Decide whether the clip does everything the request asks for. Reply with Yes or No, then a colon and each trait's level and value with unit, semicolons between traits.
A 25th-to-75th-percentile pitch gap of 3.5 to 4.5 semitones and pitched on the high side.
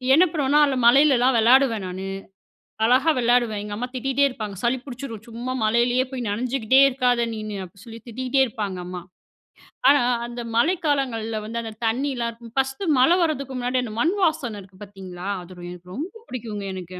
Yes: average, 3.8 semitones; high, 240 Hz